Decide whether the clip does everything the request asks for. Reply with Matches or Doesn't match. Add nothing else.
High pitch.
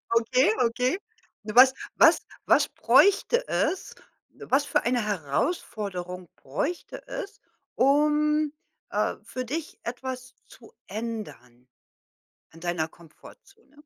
Matches